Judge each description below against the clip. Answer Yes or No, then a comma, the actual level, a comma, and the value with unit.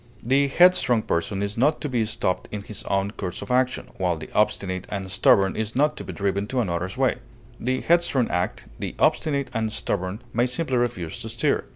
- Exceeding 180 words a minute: Yes, average, 200 wpm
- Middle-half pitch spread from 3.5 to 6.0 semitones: Yes, average, 5.0 semitones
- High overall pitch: No, low, 110 Hz